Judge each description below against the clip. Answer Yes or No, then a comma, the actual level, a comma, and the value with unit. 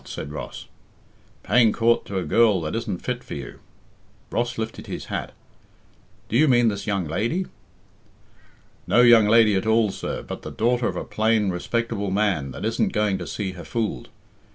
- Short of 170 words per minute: No, average, 175 wpm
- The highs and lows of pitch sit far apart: No, average, 3.6 semitones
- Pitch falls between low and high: No, low, 110 Hz